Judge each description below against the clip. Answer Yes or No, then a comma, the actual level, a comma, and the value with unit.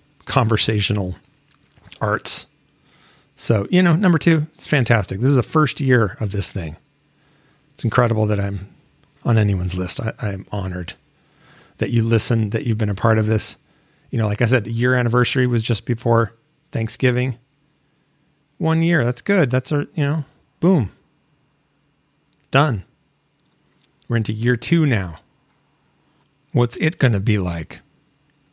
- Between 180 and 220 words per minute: No, average, 145 wpm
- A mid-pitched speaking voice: No, low, 130 Hz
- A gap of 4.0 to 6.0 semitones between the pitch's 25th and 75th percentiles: Yes, average, 4.9 semitones